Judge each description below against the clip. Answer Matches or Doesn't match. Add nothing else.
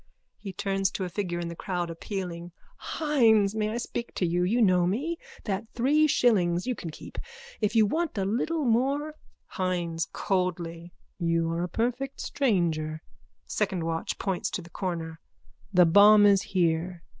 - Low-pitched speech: Doesn't match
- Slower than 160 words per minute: Doesn't match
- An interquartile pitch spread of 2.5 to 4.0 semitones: Doesn't match